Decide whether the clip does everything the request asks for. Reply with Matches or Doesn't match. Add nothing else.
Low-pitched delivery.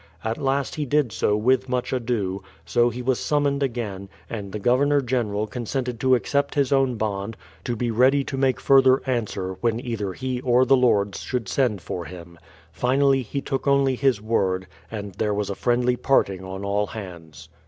Matches